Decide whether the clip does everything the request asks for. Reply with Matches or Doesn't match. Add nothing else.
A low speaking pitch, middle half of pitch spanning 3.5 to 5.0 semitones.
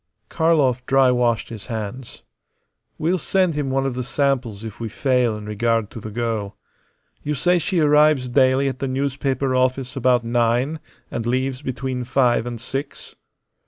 Doesn't match